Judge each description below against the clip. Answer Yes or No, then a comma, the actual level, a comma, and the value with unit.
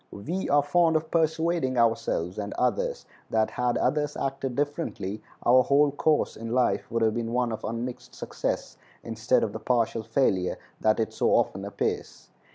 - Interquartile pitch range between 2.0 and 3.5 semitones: No, average, 4.8 semitones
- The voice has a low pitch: Yes, low, 125 Hz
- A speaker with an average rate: Yes, average, 165 wpm